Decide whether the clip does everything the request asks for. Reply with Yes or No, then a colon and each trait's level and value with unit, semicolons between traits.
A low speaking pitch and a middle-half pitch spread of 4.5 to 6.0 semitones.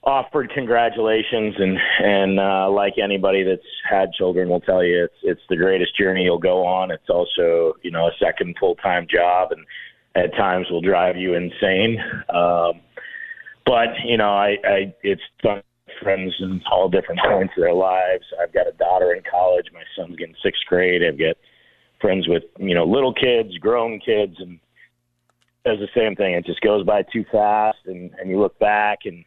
No: very low, 95 Hz; average, 3.4 semitones